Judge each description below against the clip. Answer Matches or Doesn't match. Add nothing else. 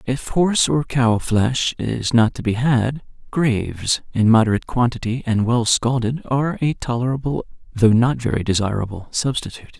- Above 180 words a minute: Doesn't match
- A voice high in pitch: Doesn't match